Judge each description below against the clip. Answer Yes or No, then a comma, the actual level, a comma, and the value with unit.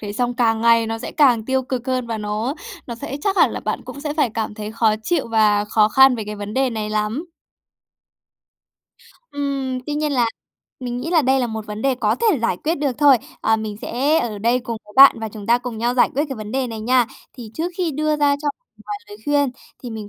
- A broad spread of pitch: No, average, 4.2 semitones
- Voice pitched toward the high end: Yes, high, 245 Hz